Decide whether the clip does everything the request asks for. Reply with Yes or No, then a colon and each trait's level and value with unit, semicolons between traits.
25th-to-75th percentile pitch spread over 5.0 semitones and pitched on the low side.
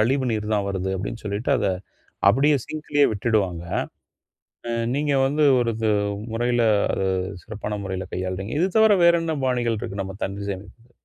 Yes: wide, 5.4 semitones; low, 110 Hz